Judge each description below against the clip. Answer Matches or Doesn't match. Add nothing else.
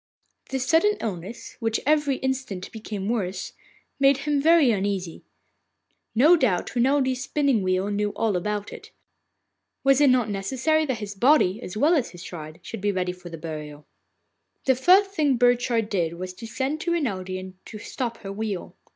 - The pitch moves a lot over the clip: Matches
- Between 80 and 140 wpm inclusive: Doesn't match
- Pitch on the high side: Matches